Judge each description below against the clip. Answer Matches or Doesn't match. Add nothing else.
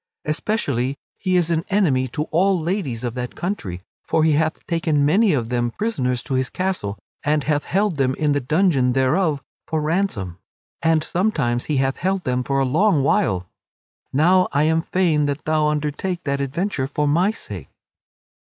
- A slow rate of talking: Doesn't match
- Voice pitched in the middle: Matches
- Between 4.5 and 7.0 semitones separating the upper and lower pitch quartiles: Matches